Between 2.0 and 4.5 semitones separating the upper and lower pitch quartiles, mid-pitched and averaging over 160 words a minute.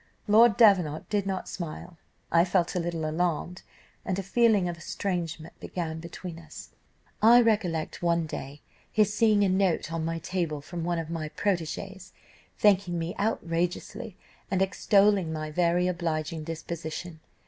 No: average, 3.0 semitones; medium, 175 Hz; average, 150 wpm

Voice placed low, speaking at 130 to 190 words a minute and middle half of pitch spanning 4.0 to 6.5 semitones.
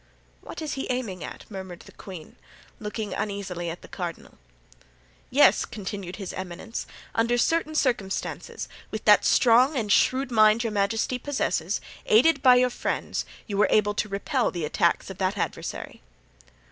No: high, 210 Hz; average, 155 wpm; average, 4.6 semitones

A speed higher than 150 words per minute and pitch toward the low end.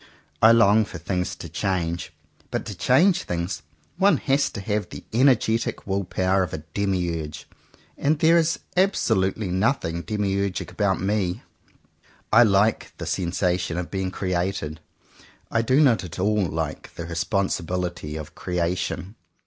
No: average, 140 wpm; very low, 95 Hz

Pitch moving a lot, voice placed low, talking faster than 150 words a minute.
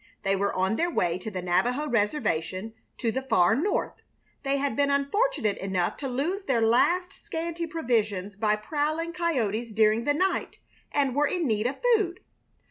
No: wide, 7.2 semitones; very high, 255 Hz; average, 170 wpm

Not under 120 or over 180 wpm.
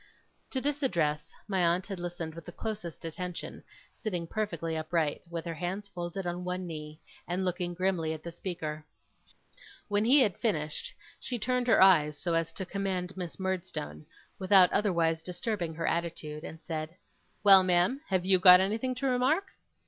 Yes: average, 170 wpm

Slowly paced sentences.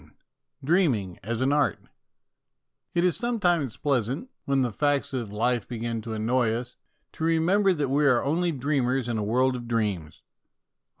No: average, 165 wpm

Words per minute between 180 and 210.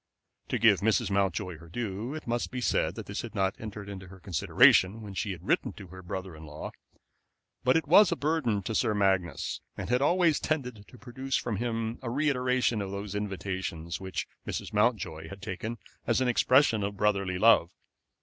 Yes: average, 195 wpm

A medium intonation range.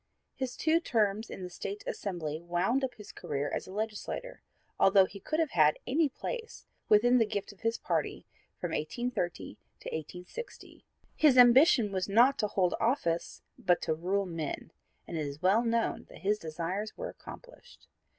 No: wide, 5.8 semitones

